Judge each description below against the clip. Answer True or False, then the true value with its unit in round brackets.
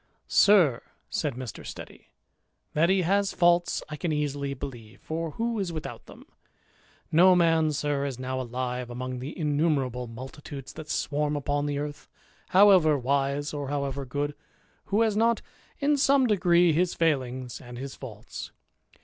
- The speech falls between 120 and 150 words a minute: False (160 wpm)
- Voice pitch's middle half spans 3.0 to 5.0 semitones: True (4.7 semitones)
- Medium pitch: True (145 Hz)